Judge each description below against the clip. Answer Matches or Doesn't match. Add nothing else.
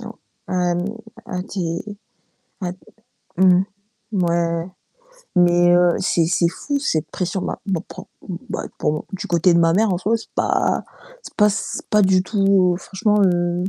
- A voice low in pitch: Doesn't match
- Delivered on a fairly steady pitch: Matches